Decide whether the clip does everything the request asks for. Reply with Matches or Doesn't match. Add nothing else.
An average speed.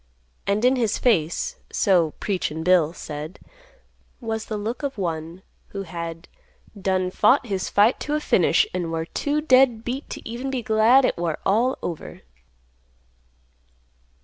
Matches